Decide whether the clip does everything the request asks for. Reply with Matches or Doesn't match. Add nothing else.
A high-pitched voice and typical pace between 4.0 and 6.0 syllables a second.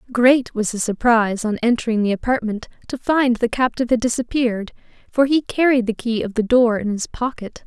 Matches